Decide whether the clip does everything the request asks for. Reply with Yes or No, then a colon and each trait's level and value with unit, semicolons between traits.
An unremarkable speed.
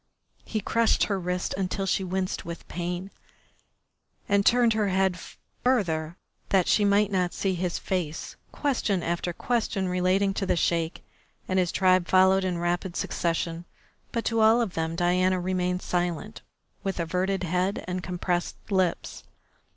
Yes: average, 150 wpm